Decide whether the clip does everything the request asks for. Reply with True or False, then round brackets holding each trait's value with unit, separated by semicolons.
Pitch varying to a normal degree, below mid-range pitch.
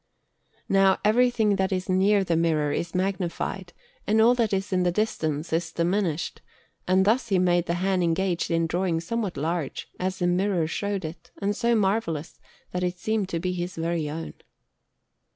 False (3.0 semitones; 185 Hz)